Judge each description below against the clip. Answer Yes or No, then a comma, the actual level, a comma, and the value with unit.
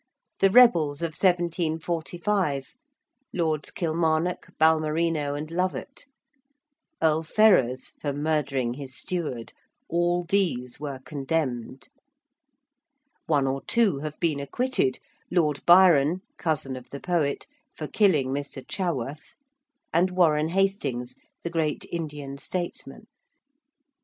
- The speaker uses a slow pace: Yes, slow, 105 wpm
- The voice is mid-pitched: Yes, medium, 155 Hz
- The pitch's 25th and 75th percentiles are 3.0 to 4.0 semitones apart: Yes, average, 3.7 semitones